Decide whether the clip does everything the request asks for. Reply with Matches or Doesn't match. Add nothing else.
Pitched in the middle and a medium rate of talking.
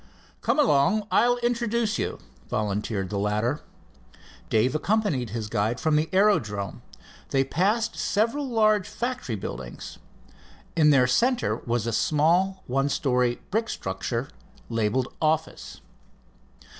Doesn't match